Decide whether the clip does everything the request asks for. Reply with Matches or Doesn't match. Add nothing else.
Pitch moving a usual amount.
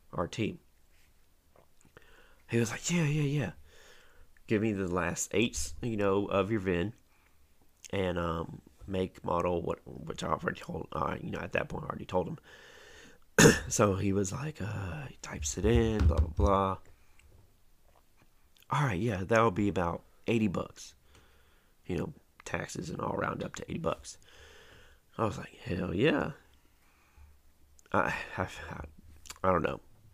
Matches